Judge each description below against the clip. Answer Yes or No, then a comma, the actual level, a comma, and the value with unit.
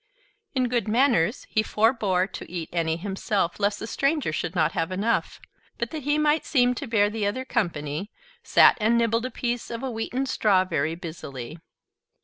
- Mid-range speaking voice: No, high, 215 Hz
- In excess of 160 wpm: Yes, average, 180 wpm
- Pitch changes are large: Yes, wide, 5.8 semitones